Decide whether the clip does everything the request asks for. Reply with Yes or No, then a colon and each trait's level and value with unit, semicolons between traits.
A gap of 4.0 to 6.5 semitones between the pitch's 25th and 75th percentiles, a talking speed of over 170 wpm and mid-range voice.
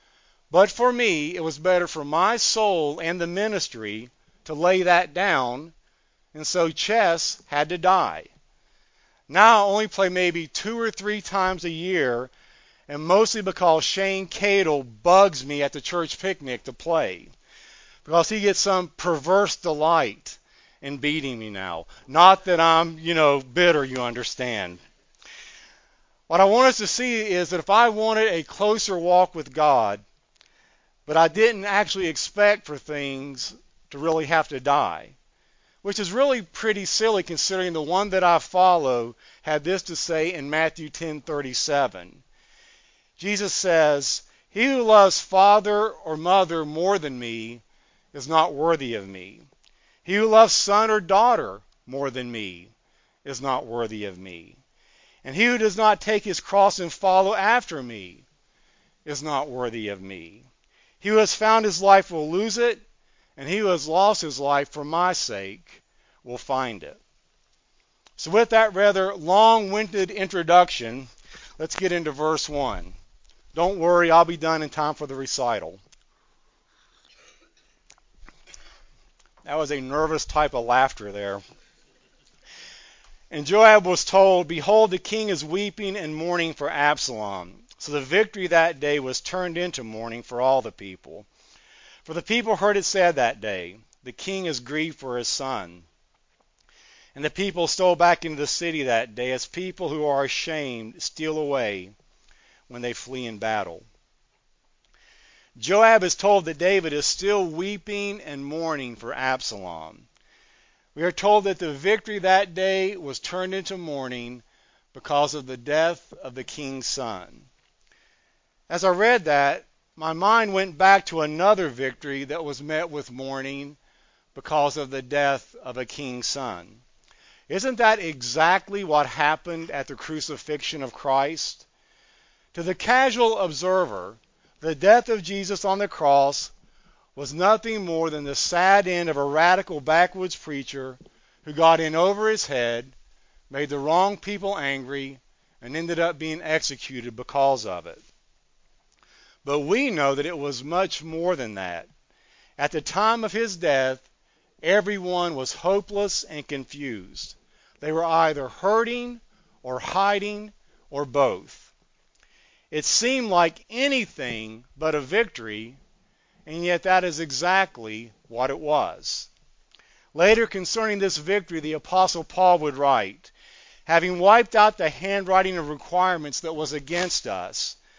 No: wide, 5.6 semitones; average, 150 wpm; medium, 165 Hz